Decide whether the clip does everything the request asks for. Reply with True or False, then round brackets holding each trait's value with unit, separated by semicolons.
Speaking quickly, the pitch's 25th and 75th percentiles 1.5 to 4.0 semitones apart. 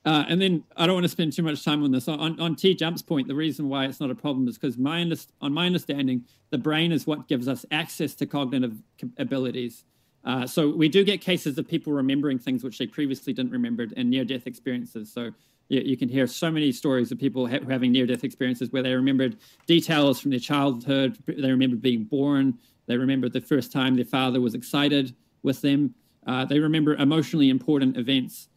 True (220 wpm; 3.1 semitones)